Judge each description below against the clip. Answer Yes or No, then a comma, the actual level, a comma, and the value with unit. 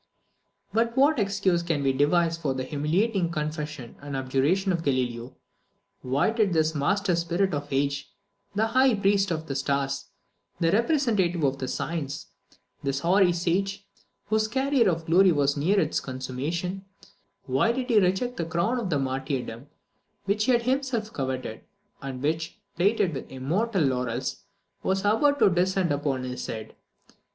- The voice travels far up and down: Yes, wide, 6.3 semitones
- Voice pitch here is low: No, medium, 170 Hz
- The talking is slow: No, average, 150 wpm